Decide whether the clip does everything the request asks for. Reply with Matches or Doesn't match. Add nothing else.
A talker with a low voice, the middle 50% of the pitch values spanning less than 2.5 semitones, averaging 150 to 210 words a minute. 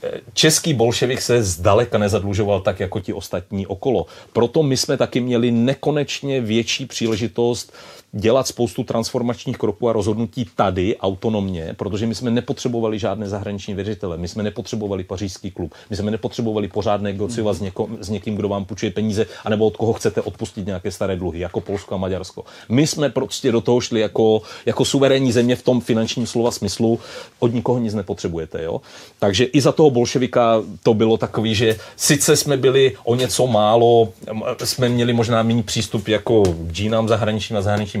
Doesn't match